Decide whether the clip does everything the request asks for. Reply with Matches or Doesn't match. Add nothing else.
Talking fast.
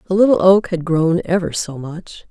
Matches